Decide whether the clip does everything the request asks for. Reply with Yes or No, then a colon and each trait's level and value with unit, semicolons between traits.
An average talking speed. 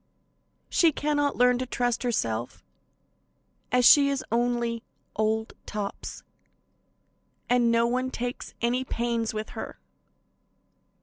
No: slow, 110 wpm